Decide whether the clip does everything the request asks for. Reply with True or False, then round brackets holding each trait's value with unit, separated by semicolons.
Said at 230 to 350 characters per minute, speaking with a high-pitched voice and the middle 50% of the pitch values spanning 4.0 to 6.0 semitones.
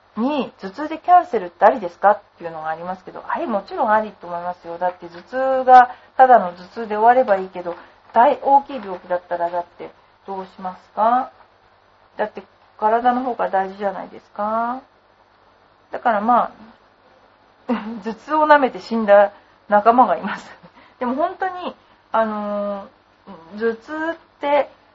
True (310 characters per minute; 220 Hz; 5.3 semitones)